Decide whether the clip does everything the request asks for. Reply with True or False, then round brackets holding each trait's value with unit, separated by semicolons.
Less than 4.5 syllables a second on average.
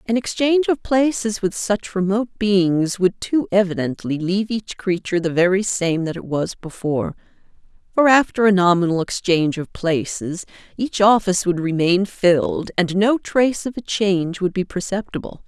False (5.0 syllables/s)